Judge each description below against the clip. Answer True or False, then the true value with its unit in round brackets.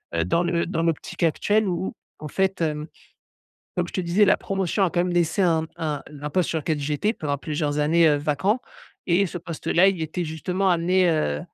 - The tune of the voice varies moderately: True (3.3 semitones)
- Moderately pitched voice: True (170 Hz)